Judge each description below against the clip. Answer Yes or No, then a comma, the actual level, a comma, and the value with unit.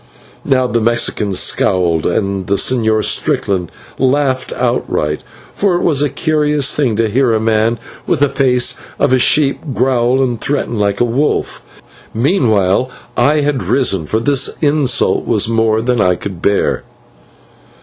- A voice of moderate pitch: No, low, 120 Hz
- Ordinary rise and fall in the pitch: Yes, average, 4.3 semitones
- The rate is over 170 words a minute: No, average, 150 wpm